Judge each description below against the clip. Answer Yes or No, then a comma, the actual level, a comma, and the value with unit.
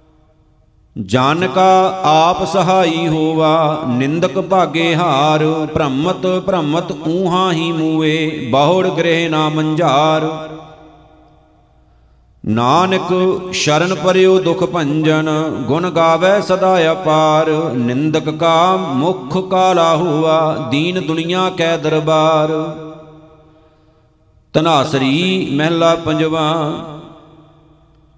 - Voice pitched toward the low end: No, medium, 160 Hz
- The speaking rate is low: Yes, slow, 80 wpm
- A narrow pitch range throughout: Yes, narrow, 2.3 semitones